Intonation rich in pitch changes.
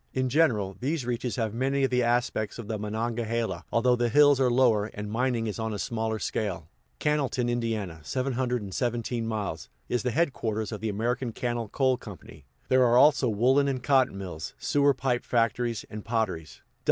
No: average, 2.9 semitones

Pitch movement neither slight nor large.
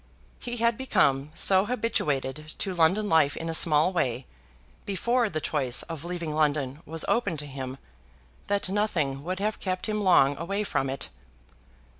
No: wide, 5.8 semitones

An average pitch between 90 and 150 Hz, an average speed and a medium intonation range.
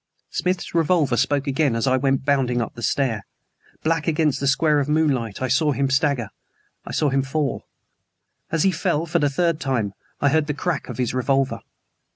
Yes: medium, 140 Hz; average, 190 wpm; average, 3.1 semitones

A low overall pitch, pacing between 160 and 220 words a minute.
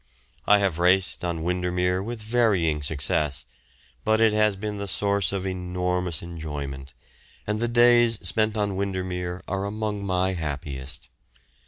No: very low, 95 Hz; average, 140 wpm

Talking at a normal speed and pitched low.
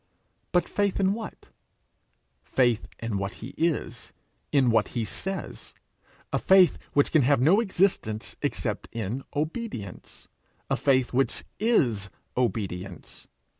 No: slow, 125 wpm; low, 130 Hz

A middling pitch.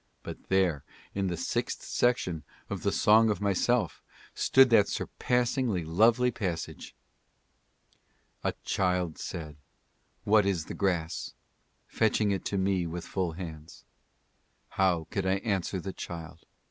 No: very low, 95 Hz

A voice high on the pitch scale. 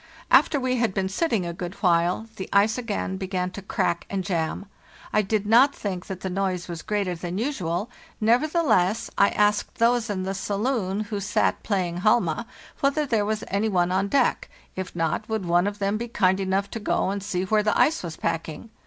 Yes: high, 200 Hz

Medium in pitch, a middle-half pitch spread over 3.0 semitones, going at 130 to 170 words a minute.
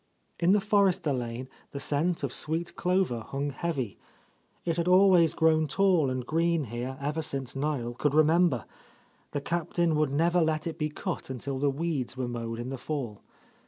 No: medium, 150 Hz; average, 4.4 semitones; average, 180 wpm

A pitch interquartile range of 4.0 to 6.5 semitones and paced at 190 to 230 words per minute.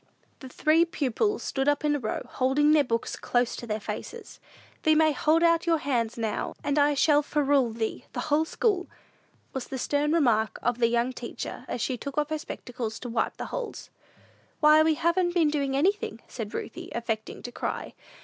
Yes: average, 4.5 semitones; average, 195 wpm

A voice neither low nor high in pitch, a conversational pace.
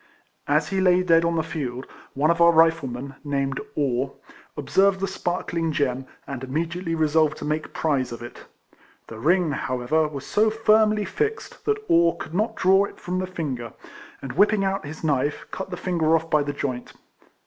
Yes: medium, 160 Hz; average, 180 wpm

